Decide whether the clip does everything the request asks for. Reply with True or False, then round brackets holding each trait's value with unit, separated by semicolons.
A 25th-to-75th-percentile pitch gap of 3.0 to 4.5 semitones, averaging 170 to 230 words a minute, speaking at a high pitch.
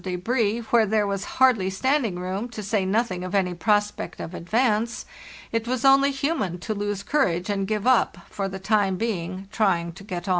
True (3.7 semitones; 195 wpm; 205 Hz)